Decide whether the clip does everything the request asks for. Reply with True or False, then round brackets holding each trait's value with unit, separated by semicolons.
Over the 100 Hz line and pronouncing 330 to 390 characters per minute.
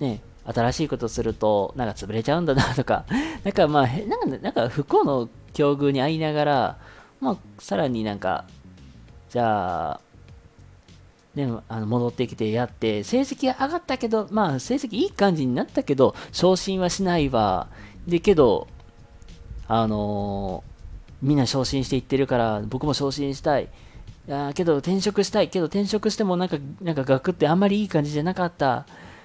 False (135 Hz; 320 characters per minute)